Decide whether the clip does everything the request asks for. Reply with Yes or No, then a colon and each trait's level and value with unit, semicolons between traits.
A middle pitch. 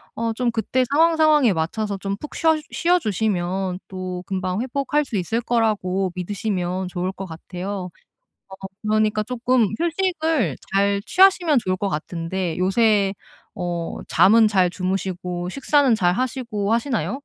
No: high, 205 Hz